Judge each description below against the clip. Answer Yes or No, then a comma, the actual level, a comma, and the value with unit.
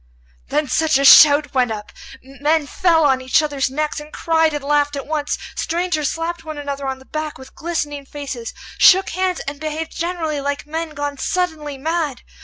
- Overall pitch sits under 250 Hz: No, very high, 295 Hz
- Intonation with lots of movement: No, narrow, 2.4 semitones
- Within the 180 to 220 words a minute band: Yes, average, 185 wpm